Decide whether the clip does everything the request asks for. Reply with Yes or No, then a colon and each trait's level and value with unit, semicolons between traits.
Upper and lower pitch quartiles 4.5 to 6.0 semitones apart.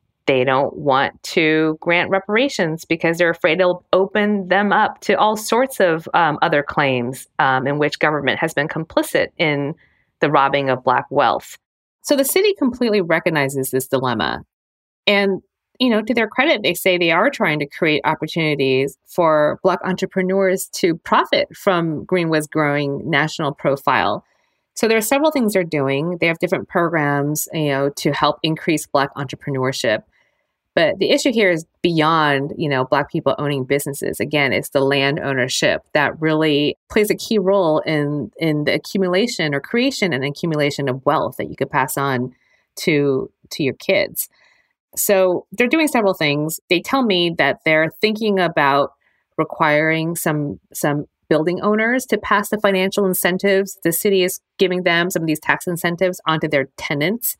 Yes: average, 5.1 semitones